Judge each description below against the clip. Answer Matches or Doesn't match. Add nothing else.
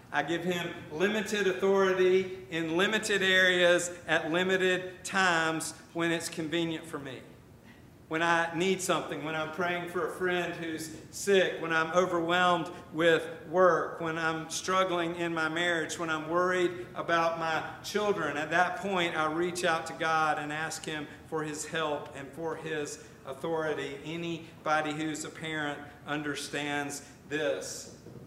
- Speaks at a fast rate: Doesn't match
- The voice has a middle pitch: Matches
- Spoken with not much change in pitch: Matches